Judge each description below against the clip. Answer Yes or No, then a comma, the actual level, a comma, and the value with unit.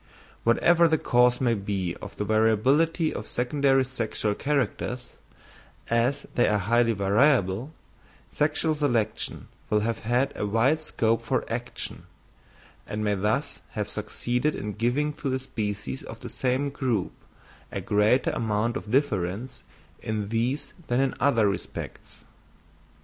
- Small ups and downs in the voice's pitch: No, average, 4.2 semitones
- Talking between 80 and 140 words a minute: Yes, slow, 135 wpm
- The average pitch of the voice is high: No, low, 120 Hz